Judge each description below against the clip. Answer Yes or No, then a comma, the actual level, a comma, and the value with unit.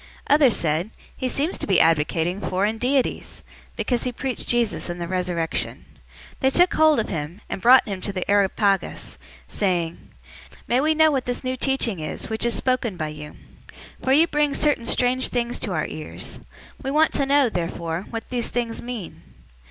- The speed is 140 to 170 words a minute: No, average, 185 wpm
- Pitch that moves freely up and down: Yes, wide, 6.6 semitones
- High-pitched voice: Yes, high, 230 Hz